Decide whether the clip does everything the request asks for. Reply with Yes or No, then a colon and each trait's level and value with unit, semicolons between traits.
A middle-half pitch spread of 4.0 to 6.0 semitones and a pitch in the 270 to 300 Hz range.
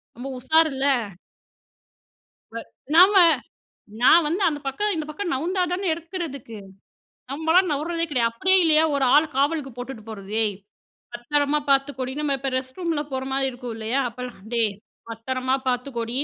Yes: average, 4.4 semitones; very high, 275 Hz